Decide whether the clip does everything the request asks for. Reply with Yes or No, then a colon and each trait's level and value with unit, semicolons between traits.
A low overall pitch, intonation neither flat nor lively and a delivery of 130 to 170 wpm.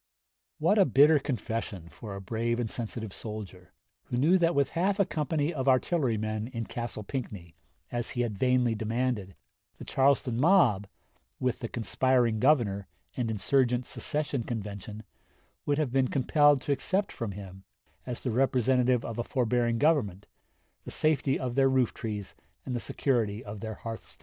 Yes: low, 120 Hz; average, 3.9 semitones; average, 160 wpm